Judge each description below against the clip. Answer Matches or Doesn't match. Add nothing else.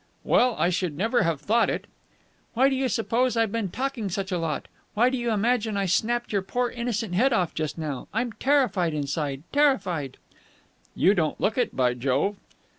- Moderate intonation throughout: Doesn't match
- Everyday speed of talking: Matches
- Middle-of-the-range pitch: Doesn't match